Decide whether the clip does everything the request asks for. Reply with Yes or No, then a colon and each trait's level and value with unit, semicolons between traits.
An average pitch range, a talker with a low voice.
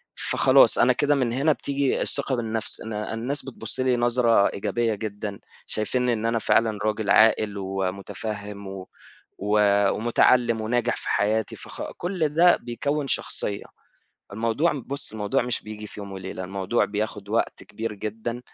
Yes: average, 3.2 semitones; low, 110 Hz